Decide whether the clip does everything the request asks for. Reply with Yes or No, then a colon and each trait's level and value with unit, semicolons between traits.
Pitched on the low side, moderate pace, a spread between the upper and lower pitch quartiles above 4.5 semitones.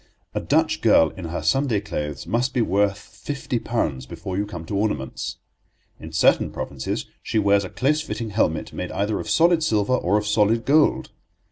Yes: low, 105 Hz; average, 180 wpm; average, 5.3 semitones